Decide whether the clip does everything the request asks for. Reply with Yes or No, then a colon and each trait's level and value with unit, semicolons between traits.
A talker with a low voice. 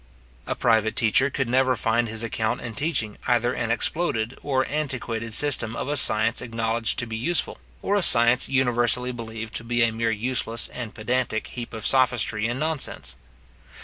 Yes: low, 120 Hz